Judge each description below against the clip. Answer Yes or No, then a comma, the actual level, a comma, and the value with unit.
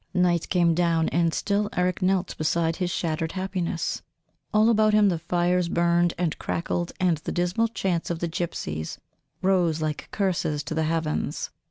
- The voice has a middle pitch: Yes, medium, 175 Hz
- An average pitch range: No, narrow, 2.1 semitones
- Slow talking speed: No, average, 165 wpm